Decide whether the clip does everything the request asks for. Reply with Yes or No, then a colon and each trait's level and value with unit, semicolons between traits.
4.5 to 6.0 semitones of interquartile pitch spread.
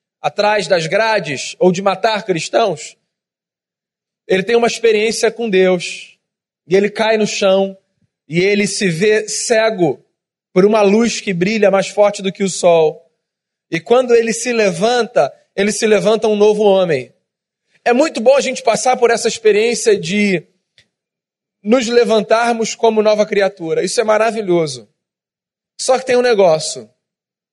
No: average, 3.1 semitones